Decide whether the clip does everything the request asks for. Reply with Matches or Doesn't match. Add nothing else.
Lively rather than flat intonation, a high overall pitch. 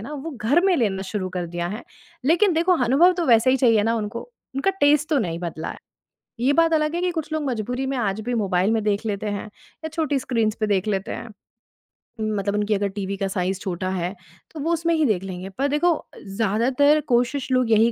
Matches